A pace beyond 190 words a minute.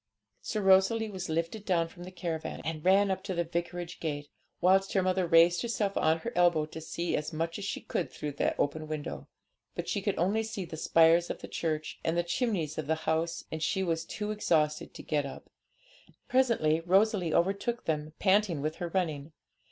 Yes: average, 200 wpm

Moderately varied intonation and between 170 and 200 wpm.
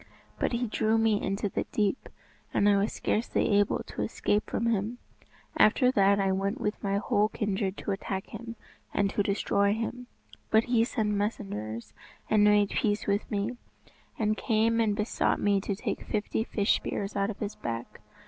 No: narrow, 1.8 semitones; average, 185 wpm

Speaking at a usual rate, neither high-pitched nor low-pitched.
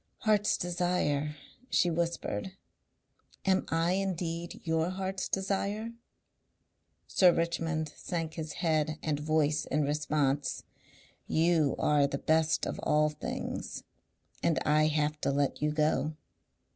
No: slow, 120 wpm; medium, 160 Hz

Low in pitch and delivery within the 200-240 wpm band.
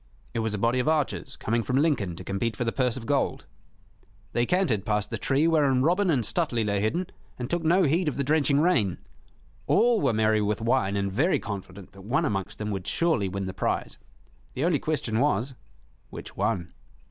Yes: low, 120 Hz; fast, 205 wpm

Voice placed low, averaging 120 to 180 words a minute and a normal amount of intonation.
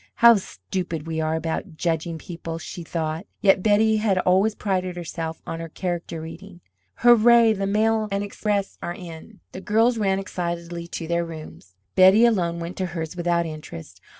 No: medium, 175 Hz; average, 170 wpm; average, 3.6 semitones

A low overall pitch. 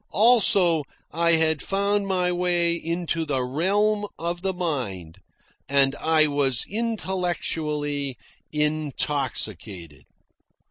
No: medium, 160 Hz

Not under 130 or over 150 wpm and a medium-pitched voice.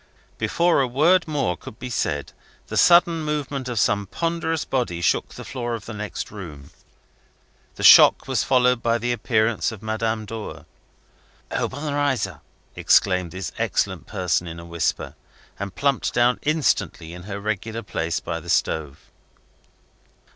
No: average, 145 wpm; low, 110 Hz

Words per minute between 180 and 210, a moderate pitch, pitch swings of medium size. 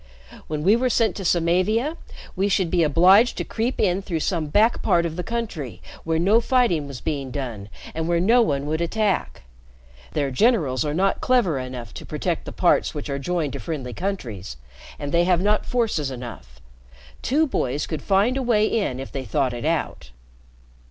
No: average, 190 wpm; medium, 170 Hz; wide, 7.1 semitones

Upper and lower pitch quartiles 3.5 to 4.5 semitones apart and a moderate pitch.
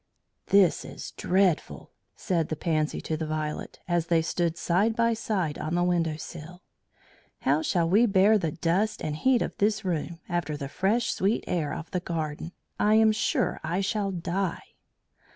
Yes: average, 3.8 semitones; medium, 175 Hz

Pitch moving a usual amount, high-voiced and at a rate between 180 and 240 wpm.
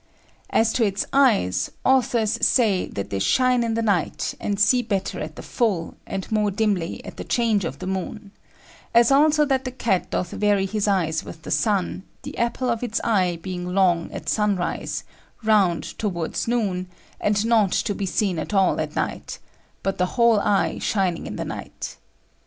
Yes: average, 3.9 semitones; high, 205 Hz; average, 185 wpm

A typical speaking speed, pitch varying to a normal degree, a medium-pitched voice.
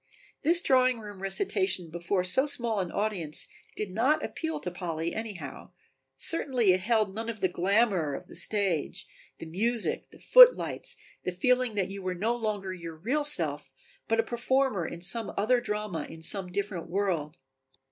No: average, 165 wpm; average, 5.0 semitones; high, 205 Hz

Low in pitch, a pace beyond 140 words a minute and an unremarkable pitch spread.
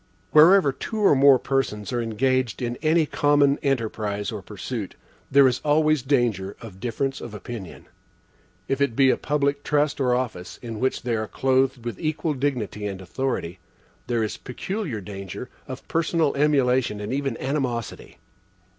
Yes: low, 130 Hz; average, 155 wpm; average, 4.2 semitones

